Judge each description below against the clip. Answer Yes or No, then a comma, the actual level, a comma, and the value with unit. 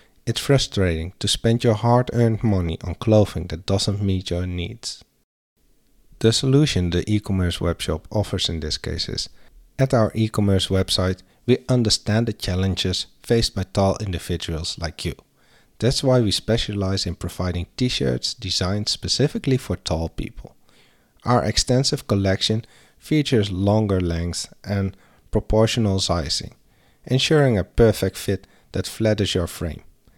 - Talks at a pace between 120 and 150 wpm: Yes, average, 140 wpm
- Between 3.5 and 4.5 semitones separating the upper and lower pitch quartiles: Yes, average, 4.1 semitones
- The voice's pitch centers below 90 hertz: No, low, 100 Hz